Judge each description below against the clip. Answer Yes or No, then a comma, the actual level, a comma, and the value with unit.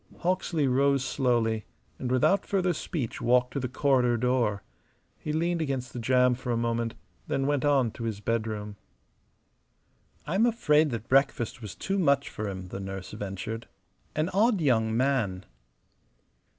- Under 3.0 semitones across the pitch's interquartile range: No, average, 4.4 semitones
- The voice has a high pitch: No, low, 125 Hz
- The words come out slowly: No, average, 150 wpm